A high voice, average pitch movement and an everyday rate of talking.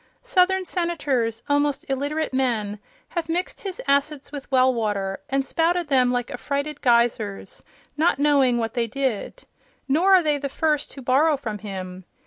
Yes: very high, 275 Hz; average, 4.5 semitones; average, 155 wpm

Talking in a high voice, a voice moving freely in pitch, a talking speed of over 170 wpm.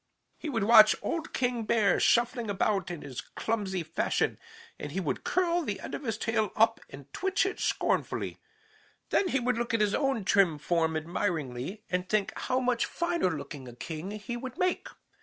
Yes: high, 215 Hz; wide, 5.8 semitones; average, 185 wpm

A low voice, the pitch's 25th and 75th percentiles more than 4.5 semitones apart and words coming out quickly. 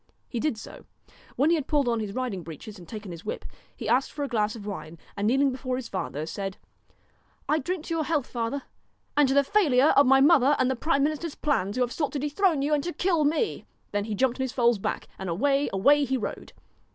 No: very high, 265 Hz; average, 5.3 semitones; fast, 245 wpm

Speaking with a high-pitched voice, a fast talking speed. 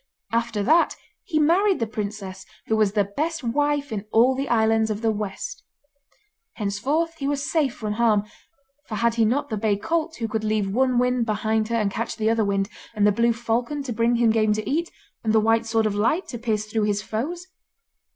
Yes: high, 225 Hz; fast, 210 wpm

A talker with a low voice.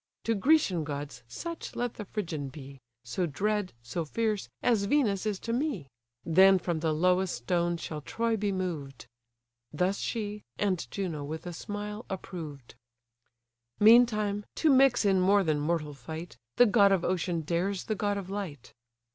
No: medium, 185 Hz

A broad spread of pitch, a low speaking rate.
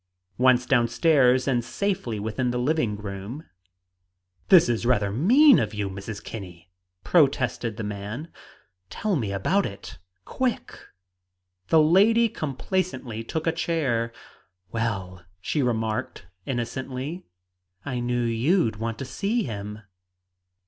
Yes: wide, 6.5 semitones; slow, 125 wpm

